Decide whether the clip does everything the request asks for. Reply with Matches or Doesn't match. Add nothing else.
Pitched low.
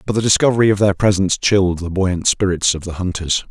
Matches